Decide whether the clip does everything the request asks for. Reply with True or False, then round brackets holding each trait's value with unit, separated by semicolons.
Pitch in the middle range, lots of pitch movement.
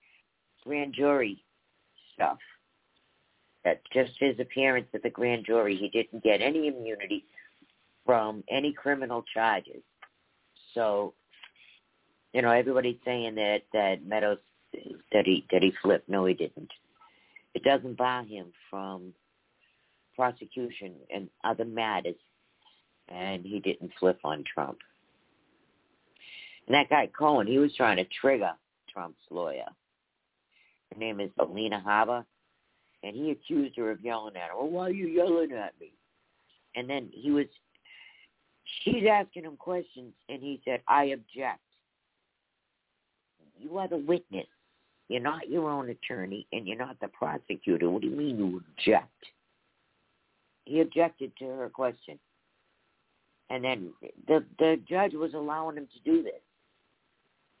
False (125 Hz; 5.7 semitones)